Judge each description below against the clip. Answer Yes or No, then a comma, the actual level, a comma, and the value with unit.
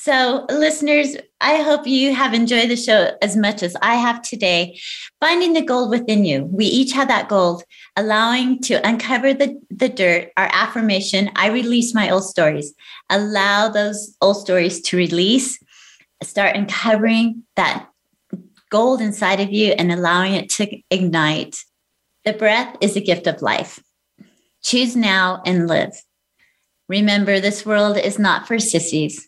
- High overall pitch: Yes, high, 210 Hz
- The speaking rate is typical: Yes, average, 150 wpm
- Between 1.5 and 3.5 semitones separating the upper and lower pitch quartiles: No, average, 4.2 semitones